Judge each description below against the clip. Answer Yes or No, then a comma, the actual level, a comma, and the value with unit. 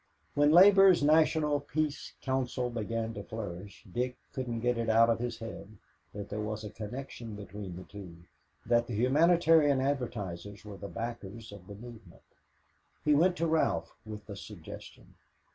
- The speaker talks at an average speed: Yes, average, 160 wpm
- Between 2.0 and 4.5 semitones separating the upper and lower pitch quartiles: No, wide, 5.5 semitones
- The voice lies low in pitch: Yes, low, 115 Hz